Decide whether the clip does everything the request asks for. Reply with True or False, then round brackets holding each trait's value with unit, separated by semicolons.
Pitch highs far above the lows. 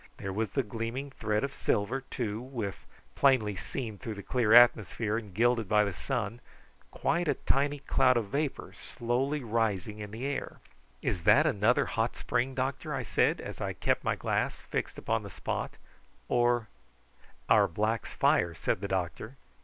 False (3.9 semitones)